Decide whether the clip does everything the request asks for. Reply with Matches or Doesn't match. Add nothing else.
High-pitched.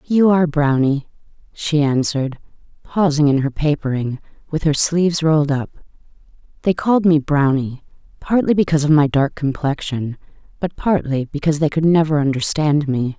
Doesn't match